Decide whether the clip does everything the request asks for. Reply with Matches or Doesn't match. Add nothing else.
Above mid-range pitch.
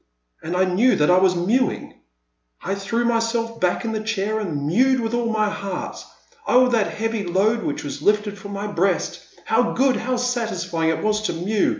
Matches